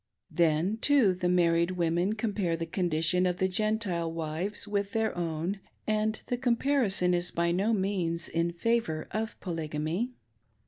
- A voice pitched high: No, medium, 180 Hz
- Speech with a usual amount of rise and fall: Yes, average, 4.2 semitones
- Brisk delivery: No, average, 145 wpm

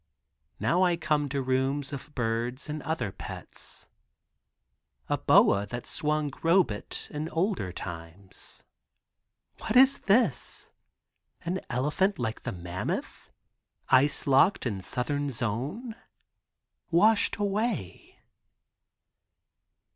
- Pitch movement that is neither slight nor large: No, wide, 6.7 semitones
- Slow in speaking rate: Yes, slow, 100 wpm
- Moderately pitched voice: Yes, medium, 145 Hz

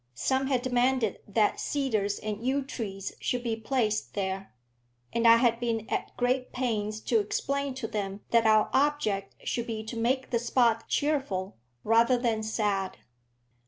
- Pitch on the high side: Yes, high, 230 Hz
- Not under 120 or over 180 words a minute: Yes, average, 160 wpm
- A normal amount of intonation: Yes, average, 3.1 semitones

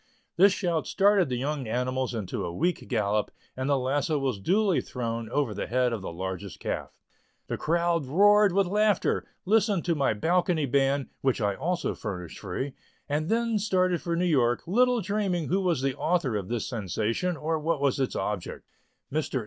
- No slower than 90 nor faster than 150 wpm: No, average, 180 wpm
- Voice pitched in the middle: Yes, medium, 145 Hz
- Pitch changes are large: Yes, wide, 7.0 semitones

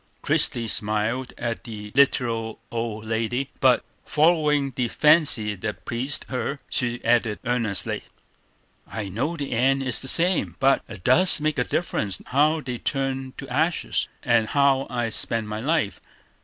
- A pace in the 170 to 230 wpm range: No, average, 150 wpm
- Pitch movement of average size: Yes, average, 3.7 semitones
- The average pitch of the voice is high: No, low, 125 Hz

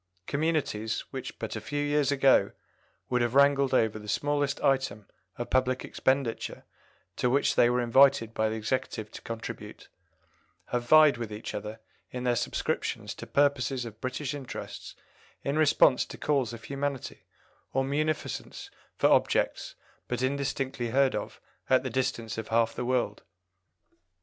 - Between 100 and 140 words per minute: No, average, 150 wpm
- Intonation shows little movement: No, average, 3.3 semitones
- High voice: No, low, 130 Hz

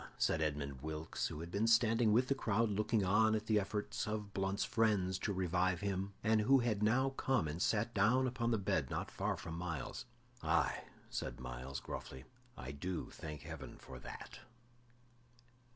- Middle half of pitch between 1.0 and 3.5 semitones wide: No, wide, 5.4 semitones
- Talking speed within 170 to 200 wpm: Yes, average, 175 wpm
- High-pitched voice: No, low, 100 Hz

